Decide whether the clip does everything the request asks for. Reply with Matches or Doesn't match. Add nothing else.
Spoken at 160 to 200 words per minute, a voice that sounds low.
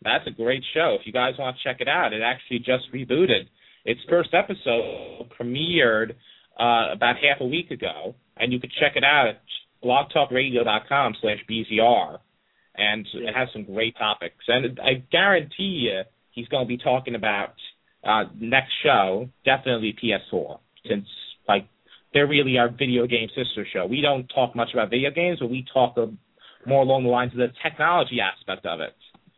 Matches